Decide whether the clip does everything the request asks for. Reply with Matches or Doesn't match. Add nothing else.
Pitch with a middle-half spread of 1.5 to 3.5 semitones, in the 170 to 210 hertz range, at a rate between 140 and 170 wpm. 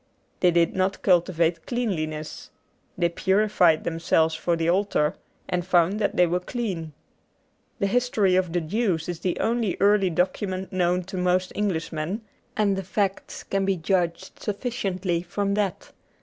Matches